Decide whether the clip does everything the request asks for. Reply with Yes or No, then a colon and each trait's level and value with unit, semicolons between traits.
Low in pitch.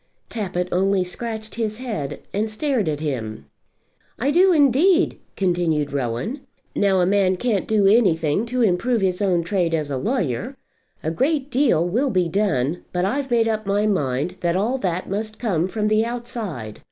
No: high, 200 Hz